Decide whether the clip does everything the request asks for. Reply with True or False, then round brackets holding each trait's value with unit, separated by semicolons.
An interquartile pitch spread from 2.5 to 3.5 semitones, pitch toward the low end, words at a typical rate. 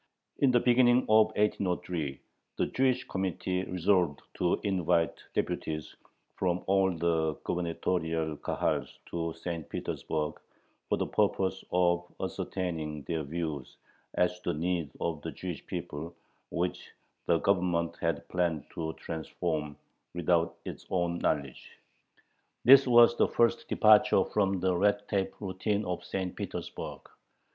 False (2.9 semitones; 90 Hz; 130 wpm)